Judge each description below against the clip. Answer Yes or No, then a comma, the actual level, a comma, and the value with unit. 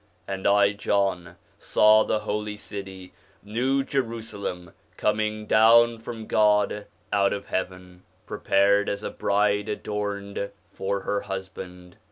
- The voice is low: Yes, low, 100 Hz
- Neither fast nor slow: No, slow, 120 wpm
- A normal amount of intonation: No, narrow, 1.7 semitones